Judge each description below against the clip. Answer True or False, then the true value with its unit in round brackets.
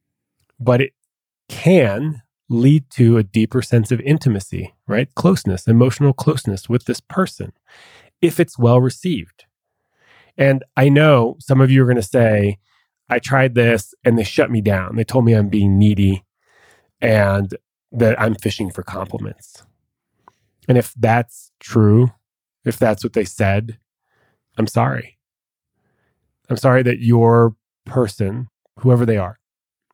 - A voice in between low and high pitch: False (120 Hz)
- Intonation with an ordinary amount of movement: True (3.1 semitones)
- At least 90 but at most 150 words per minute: True (140 wpm)